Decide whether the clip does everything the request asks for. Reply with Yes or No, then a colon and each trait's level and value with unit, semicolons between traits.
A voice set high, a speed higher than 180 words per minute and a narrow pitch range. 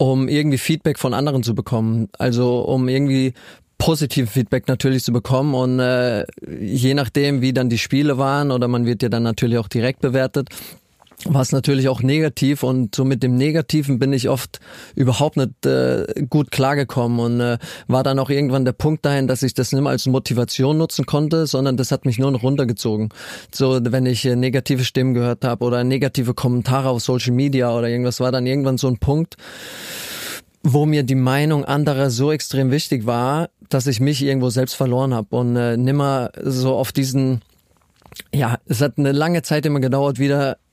No: low, 130 Hz; fast, 190 wpm; narrow, 2.1 semitones